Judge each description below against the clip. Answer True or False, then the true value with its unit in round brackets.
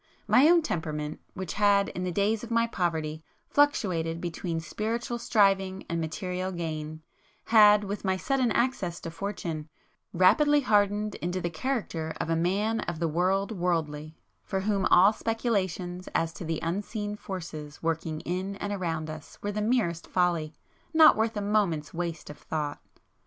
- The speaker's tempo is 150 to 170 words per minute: True (160 wpm)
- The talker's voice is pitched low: False (185 Hz)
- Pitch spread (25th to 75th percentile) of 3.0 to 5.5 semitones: True (4.2 semitones)